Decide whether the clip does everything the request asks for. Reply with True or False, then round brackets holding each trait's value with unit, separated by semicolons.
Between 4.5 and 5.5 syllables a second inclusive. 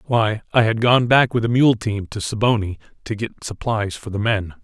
True (4.9 syllables/s)